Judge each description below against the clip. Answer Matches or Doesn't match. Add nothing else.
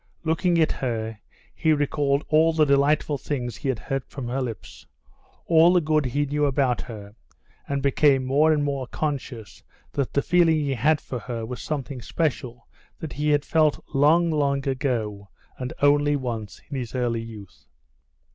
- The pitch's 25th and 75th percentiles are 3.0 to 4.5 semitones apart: Matches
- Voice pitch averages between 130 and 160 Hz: Matches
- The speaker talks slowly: Doesn't match